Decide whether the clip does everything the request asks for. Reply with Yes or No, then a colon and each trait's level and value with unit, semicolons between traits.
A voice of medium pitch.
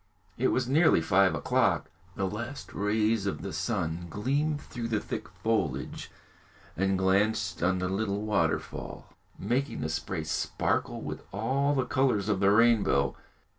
No: low, 105 Hz